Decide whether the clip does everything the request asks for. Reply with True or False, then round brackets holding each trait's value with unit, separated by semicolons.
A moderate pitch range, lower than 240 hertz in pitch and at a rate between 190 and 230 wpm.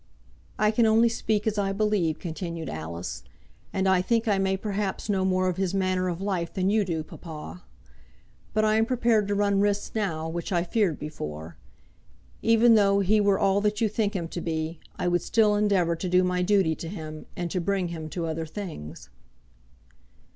True (3.6 semitones; 190 Hz; 195 wpm)